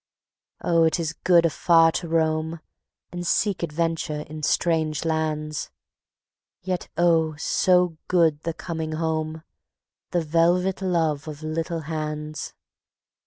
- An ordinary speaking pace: No, slow, 120 wpm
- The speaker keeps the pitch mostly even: Yes, narrow, 1.5 semitones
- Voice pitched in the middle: Yes, medium, 160 Hz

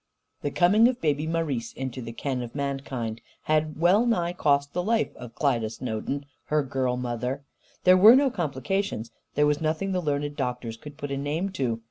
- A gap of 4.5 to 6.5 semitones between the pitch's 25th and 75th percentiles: Yes, wide, 5.4 semitones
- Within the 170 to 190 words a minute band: Yes, average, 185 wpm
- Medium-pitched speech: Yes, medium, 145 Hz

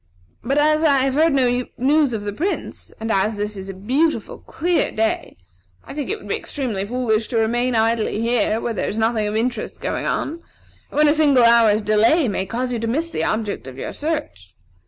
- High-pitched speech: Yes, high, 235 Hz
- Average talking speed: No, fast, 215 wpm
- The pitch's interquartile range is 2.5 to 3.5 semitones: No, average, 5.0 semitones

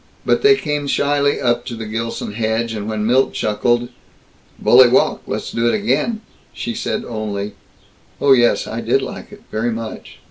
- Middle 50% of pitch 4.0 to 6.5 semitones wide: No, average, 3.2 semitones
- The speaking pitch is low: Yes, low, 120 Hz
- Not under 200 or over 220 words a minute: No, average, 175 wpm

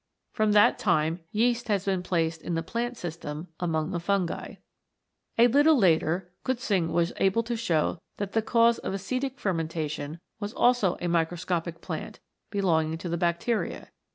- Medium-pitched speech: Yes, medium, 180 Hz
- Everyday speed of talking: Yes, average, 160 wpm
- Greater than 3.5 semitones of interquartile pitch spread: Yes, average, 5.2 semitones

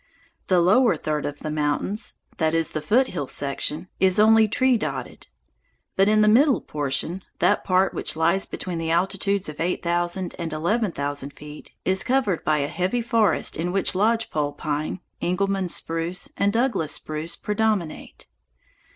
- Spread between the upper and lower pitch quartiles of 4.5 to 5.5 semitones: Yes, average, 5.1 semitones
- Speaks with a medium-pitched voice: Yes, medium, 180 Hz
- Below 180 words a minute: Yes, average, 160 wpm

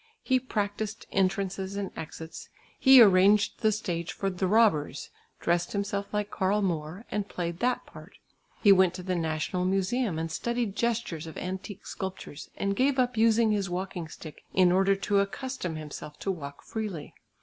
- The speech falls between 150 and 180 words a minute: Yes, average, 165 wpm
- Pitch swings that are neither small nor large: Yes, average, 3.3 semitones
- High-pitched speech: Yes, high, 195 Hz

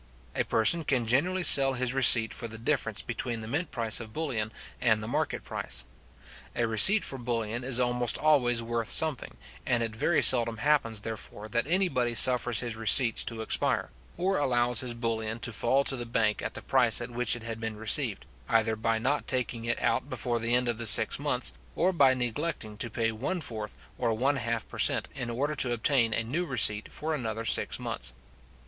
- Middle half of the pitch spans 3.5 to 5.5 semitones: No, average, 2.8 semitones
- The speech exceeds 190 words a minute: Yes, average, 200 wpm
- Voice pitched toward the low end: Yes, low, 120 Hz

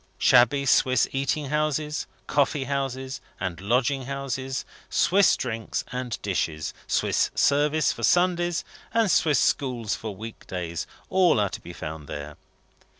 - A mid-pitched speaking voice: No, low, 130 Hz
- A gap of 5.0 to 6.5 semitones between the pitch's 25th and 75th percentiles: Yes, wide, 5.6 semitones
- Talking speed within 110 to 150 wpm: Yes, slow, 135 wpm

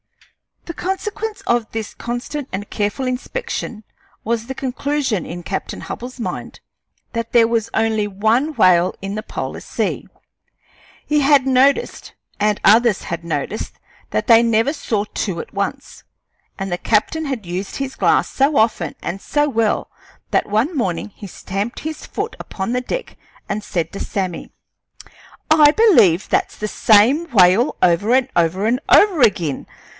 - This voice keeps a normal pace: Yes, average, 155 wpm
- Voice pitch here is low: No, high, 225 Hz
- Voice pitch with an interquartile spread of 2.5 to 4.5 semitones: No, wide, 5.5 semitones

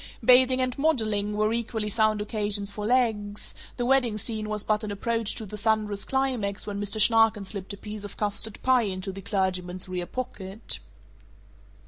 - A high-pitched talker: Yes, high, 215 Hz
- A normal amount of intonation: No, narrow, 2.2 semitones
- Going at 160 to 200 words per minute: Yes, average, 170 wpm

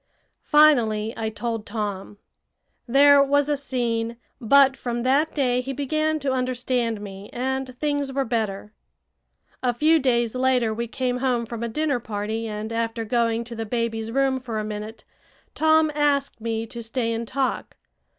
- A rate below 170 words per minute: Yes, average, 160 wpm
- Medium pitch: No, high, 240 Hz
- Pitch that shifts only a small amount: No, average, 3.2 semitones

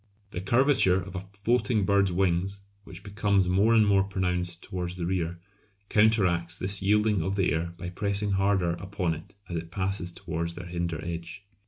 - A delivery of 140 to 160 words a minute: No, average, 175 wpm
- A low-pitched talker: Yes, very low, 95 Hz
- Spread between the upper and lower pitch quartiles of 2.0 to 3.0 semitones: Yes, narrow, 2.5 semitones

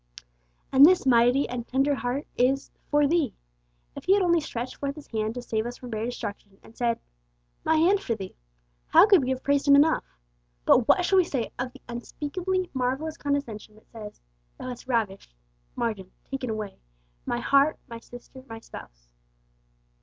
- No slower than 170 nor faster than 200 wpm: Yes, average, 180 wpm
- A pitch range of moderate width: Yes, average, 4.0 semitones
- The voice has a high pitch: Yes, very high, 255 Hz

